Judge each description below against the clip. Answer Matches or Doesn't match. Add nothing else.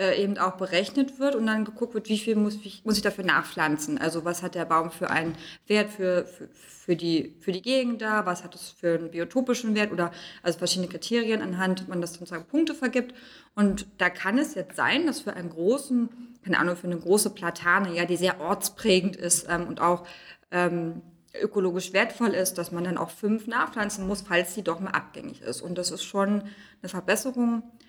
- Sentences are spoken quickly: Matches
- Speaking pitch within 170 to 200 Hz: Matches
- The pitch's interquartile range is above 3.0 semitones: Matches